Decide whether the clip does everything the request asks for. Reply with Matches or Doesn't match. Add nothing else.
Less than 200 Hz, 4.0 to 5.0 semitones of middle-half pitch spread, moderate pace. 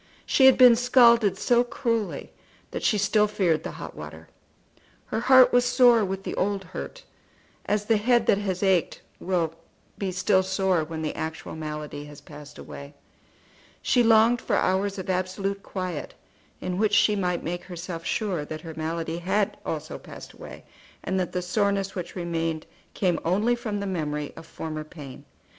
Matches